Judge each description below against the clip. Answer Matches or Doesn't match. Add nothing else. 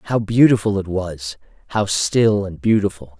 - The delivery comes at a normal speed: Matches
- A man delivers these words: Matches